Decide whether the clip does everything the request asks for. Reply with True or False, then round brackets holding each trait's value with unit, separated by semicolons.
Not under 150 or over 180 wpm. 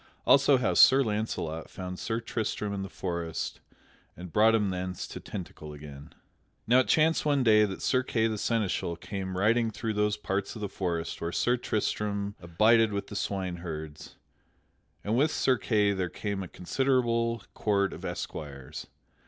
True (165 wpm)